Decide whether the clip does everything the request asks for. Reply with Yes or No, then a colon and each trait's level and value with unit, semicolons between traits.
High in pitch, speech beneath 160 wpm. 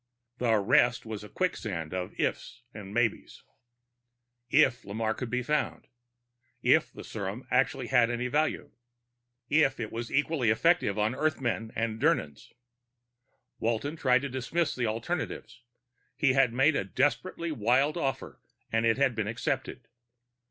No: low, 125 Hz; average, 140 wpm